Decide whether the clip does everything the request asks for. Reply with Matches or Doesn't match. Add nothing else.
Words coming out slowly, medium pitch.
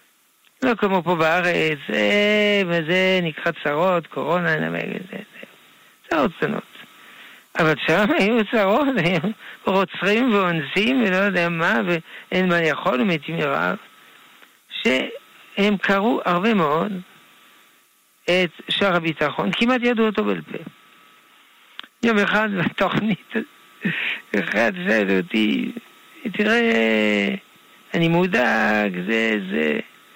Matches